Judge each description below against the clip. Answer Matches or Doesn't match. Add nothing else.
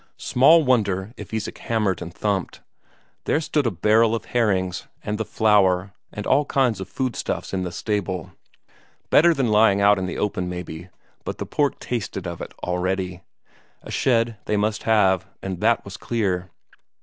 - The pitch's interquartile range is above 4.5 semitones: Doesn't match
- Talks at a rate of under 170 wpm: Doesn't match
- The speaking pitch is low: Matches